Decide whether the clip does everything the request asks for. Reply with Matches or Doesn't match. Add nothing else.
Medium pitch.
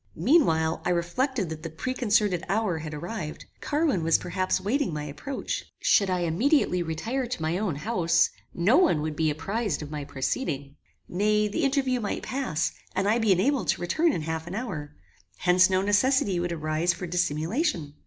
Matches